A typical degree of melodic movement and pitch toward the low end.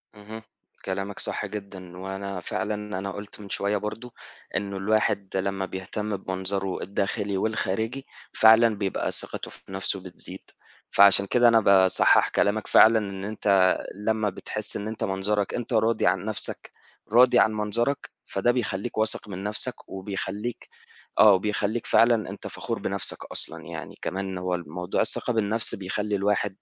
No: narrow, 2.1 semitones; low, 100 Hz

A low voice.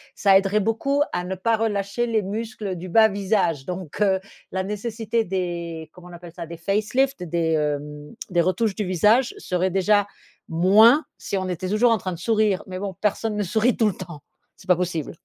No: high, 195 Hz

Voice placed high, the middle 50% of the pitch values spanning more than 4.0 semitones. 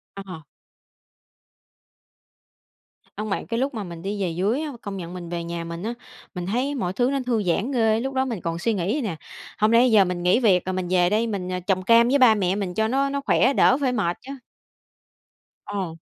Yes: high, 205 Hz; average, 5.1 semitones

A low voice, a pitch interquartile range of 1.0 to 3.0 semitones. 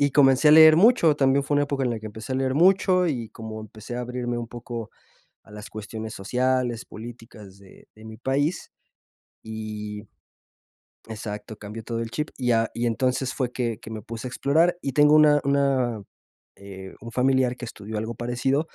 No: low, 120 Hz; average, 3.9 semitones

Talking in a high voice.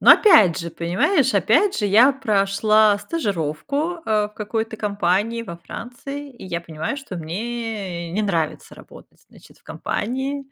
Yes: high, 215 Hz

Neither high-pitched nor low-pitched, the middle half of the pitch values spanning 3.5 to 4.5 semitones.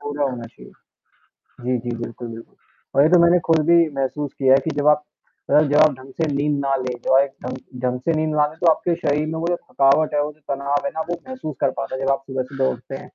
No: medium, 145 Hz; average, 2.8 semitones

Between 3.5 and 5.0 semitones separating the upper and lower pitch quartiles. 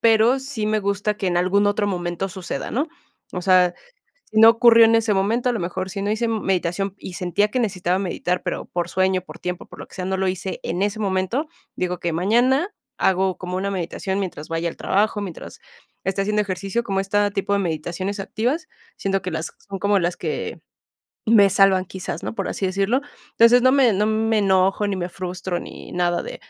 No: average, 2.9 semitones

